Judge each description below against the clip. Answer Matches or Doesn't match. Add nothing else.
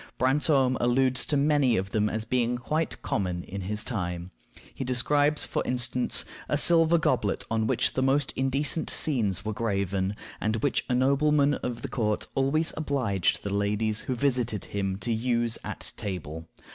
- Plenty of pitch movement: Doesn't match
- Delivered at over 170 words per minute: Doesn't match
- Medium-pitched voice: Doesn't match